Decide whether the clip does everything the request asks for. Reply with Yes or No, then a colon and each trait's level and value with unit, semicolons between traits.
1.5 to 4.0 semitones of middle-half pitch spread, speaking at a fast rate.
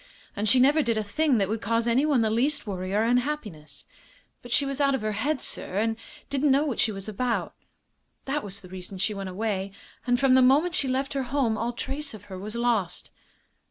No: average, 4.8 semitones; fast, 225 wpm